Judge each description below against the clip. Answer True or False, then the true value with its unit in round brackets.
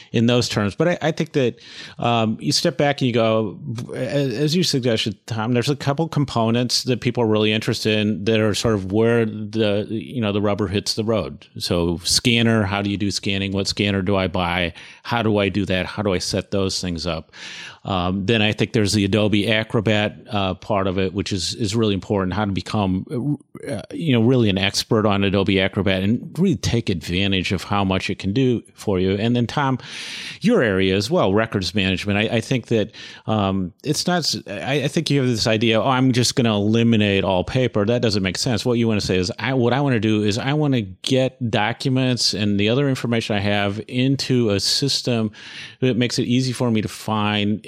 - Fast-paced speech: True (225 wpm)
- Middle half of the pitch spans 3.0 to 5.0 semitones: True (3.6 semitones)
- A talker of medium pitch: False (110 Hz)